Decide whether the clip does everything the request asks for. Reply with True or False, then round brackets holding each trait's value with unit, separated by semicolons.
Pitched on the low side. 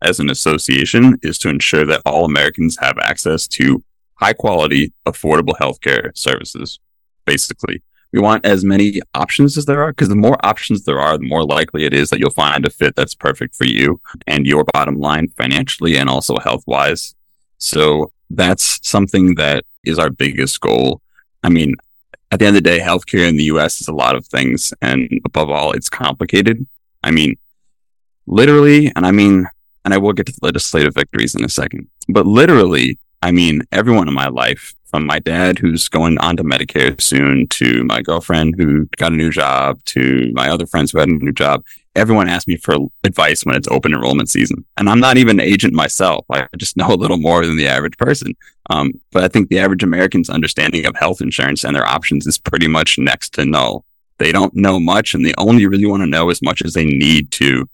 True (85 Hz)